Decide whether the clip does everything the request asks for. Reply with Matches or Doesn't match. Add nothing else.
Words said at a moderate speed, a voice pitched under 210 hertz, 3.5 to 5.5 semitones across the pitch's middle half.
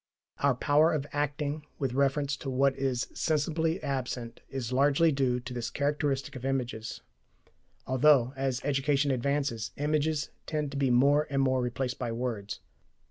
Doesn't match